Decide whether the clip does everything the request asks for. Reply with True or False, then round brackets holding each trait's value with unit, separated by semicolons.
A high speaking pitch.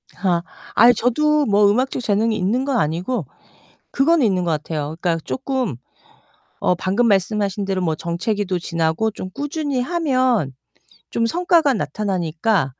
True (210 Hz)